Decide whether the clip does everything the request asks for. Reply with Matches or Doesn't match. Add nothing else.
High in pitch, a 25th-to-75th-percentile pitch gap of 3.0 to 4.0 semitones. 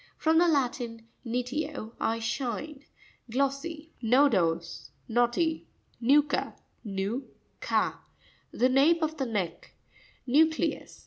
Doesn't match